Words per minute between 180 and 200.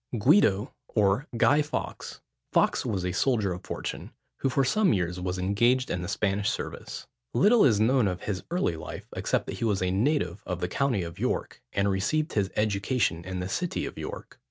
Yes: average, 195 wpm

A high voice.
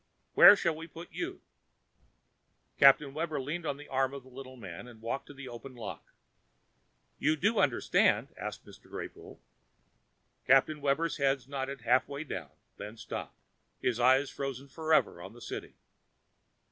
No: low, 135 Hz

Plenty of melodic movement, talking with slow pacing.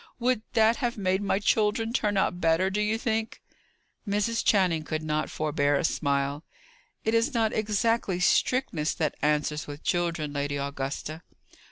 No: wide, 6.5 semitones; average, 155 wpm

